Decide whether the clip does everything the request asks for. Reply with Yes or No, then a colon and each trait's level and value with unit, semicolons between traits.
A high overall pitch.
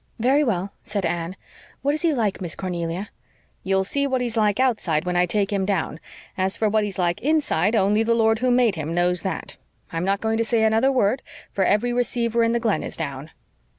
Yes: high, 210 Hz